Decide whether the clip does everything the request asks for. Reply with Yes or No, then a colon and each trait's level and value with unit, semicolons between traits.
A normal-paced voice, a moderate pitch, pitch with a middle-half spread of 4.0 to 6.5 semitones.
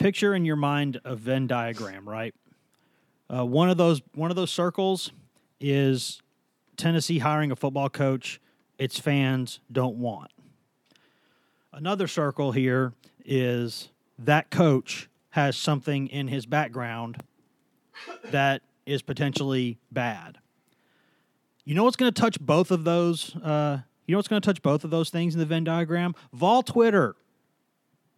Yes: average, 145 wpm; medium, 145 Hz; average, 4.5 semitones